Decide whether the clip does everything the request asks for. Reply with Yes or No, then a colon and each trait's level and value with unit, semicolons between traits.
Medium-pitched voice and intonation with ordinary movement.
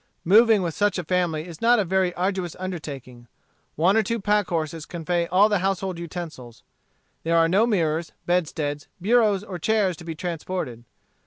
Yes: medium, 180 Hz; average, 3.3 semitones